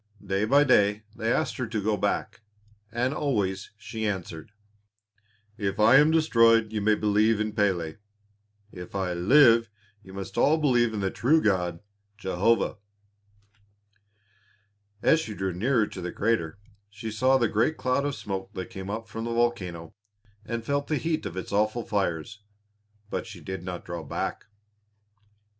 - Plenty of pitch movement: No, average, 3.7 semitones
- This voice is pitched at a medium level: No, low, 105 Hz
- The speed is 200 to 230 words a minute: No, average, 160 wpm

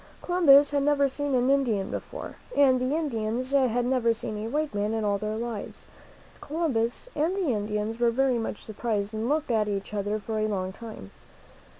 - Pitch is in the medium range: No, high, 235 Hz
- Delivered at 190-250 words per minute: Yes, average, 200 wpm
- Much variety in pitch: No, average, 4.6 semitones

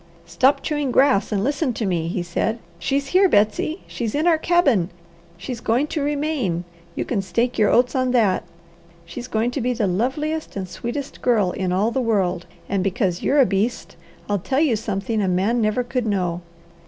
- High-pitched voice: Yes, high, 230 Hz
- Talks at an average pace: Yes, average, 190 wpm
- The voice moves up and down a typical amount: No, wide, 5.7 semitones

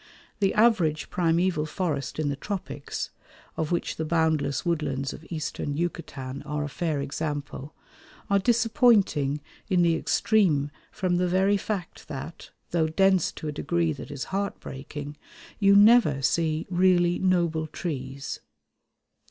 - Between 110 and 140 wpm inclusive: Yes, slow, 135 wpm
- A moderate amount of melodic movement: Yes, average, 4.2 semitones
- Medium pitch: Yes, medium, 165 Hz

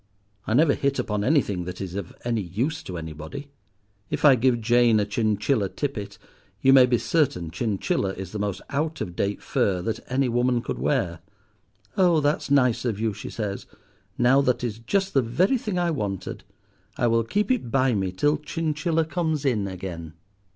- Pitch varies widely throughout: Yes, wide, 6.1 semitones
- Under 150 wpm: No, average, 185 wpm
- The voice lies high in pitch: No, low, 120 Hz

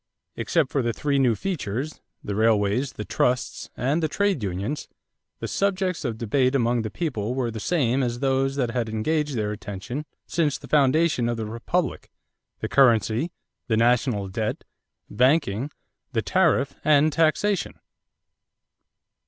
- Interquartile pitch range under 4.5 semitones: No, average, 5.2 semitones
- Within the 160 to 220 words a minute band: No, average, 145 wpm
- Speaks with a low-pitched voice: Yes, low, 130 Hz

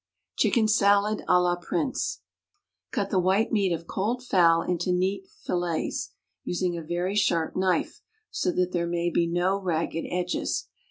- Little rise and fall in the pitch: Yes, narrow, 2.3 semitones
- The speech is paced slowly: No, average, 155 wpm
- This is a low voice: No, medium, 180 Hz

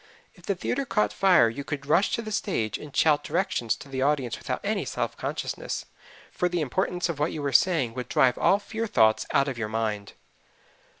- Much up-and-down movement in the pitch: Yes, wide, 6.9 semitones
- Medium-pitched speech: Yes, medium, 150 Hz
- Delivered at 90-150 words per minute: No, fast, 205 wpm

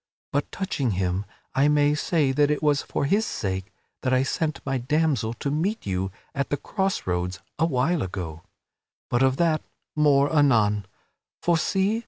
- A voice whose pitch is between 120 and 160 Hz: Yes, medium, 140 Hz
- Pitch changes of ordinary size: No, wide, 6.7 semitones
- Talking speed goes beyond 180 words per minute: No, average, 165 wpm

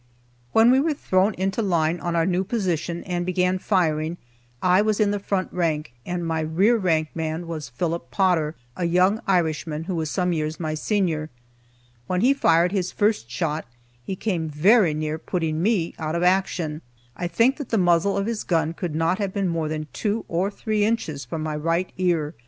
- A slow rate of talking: No, average, 195 wpm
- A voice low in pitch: No, medium, 175 Hz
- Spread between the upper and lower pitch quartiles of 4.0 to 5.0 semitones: No, average, 3.5 semitones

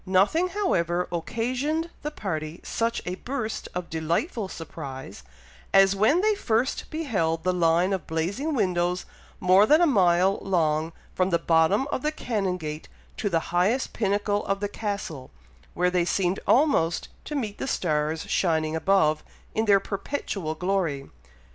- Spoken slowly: No, average, 150 wpm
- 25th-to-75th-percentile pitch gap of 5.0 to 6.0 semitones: Yes, average, 5.3 semitones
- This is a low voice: No, high, 190 Hz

